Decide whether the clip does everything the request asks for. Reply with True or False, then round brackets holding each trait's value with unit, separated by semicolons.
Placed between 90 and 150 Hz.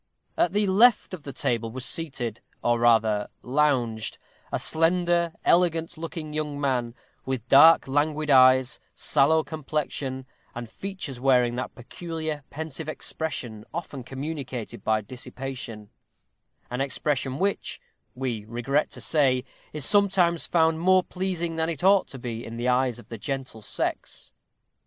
True (140 Hz)